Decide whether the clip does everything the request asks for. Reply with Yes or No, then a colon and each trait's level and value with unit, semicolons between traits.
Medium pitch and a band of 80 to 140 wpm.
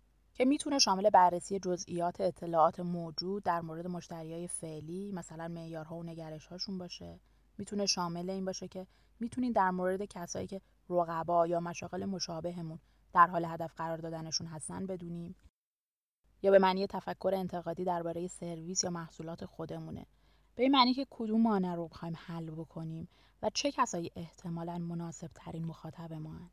No: medium, 175 Hz; average, 150 wpm